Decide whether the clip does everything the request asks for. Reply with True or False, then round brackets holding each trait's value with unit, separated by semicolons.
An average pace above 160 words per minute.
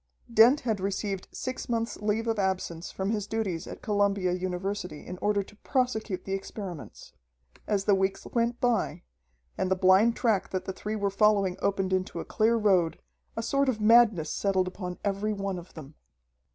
True (180 wpm)